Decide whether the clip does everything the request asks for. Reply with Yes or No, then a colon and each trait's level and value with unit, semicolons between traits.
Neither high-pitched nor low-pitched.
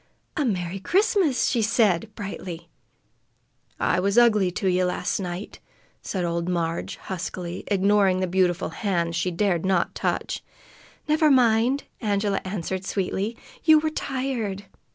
No: high, 195 Hz